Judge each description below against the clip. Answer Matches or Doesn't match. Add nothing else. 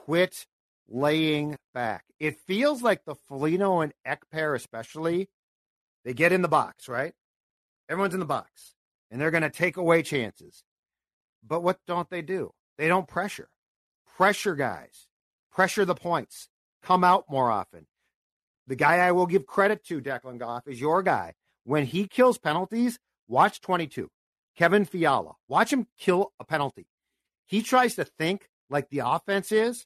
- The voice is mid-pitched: Matches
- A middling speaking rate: Matches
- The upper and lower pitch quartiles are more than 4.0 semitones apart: Matches